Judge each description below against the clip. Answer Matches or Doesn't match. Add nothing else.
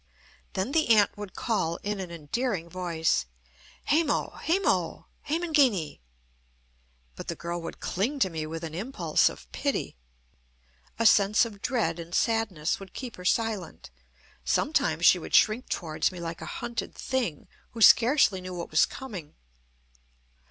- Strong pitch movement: Matches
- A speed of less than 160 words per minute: Matches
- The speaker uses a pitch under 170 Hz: Doesn't match